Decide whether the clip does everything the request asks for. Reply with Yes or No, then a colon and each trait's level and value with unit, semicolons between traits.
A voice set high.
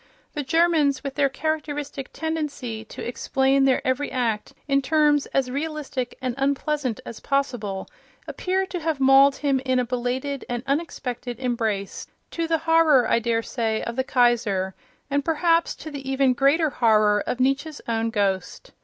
Yes: very high, 270 Hz